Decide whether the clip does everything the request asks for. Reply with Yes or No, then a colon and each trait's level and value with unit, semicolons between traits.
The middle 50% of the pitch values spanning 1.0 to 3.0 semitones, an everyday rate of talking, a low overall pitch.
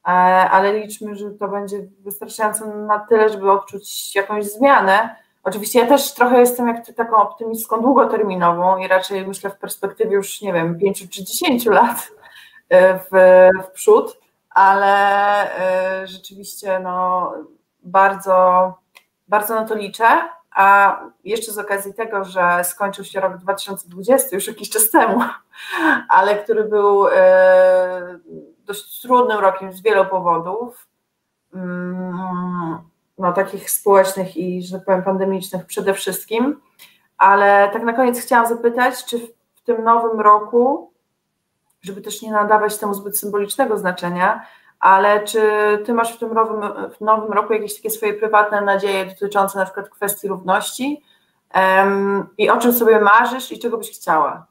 No: narrow, 2.5 semitones; average, 140 wpm; high, 200 Hz